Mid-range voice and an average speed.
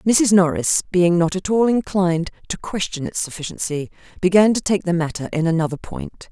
Yes: medium, 175 Hz; average, 180 wpm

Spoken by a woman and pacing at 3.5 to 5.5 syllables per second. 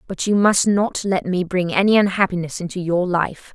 Yes: female; 5.1 syllables/s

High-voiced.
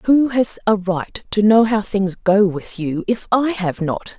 Yes: high, 205 Hz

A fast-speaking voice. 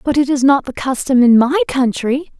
Yes: fast, 225 wpm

